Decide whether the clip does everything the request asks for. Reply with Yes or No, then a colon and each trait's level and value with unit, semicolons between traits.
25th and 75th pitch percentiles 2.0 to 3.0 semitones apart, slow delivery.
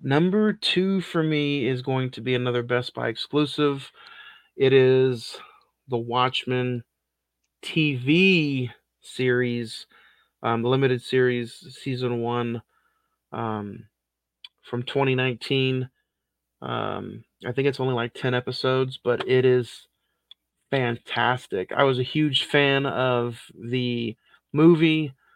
Yes: narrow, 2.4 semitones; slow, 110 wpm